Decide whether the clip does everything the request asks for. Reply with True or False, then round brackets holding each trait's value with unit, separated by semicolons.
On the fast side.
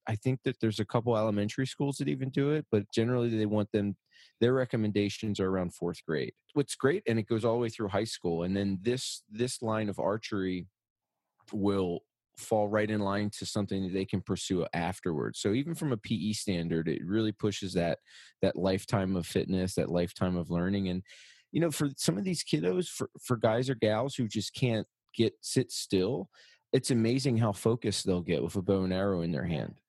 True (210 wpm)